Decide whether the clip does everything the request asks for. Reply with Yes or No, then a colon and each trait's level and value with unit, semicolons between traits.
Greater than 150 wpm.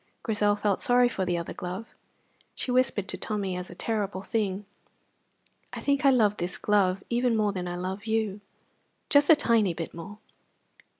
Yes: average, 175 wpm